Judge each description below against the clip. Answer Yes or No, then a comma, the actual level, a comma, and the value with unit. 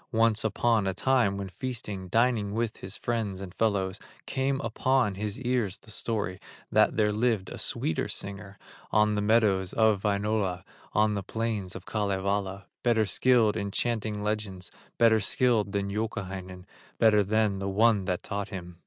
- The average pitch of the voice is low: Yes, low, 105 Hz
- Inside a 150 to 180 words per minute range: Yes, average, 160 wpm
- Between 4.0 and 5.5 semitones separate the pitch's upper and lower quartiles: No, narrow, 2.5 semitones